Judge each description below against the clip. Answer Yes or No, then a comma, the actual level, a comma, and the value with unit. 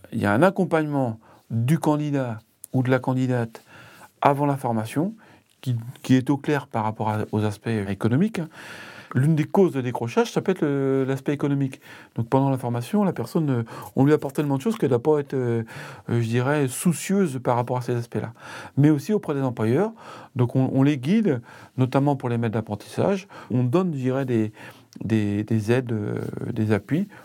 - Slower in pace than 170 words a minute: No, average, 185 wpm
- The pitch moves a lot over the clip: No, average, 4.3 semitones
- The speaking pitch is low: Yes, low, 130 Hz